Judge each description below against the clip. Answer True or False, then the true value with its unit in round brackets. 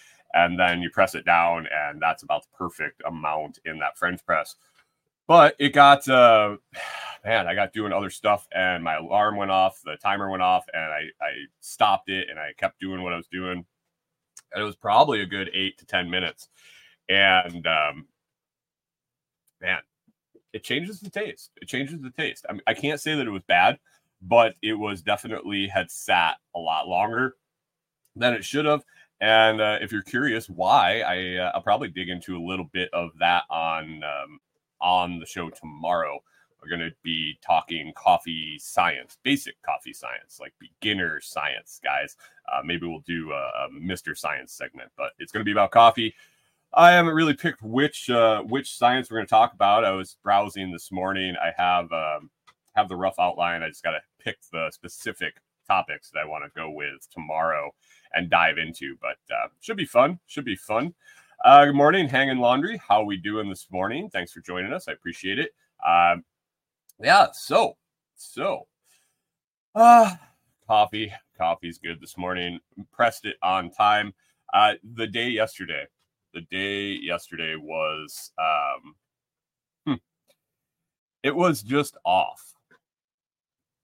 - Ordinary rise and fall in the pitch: False (6.6 semitones)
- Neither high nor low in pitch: False (105 Hz)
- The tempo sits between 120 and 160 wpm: False (170 wpm)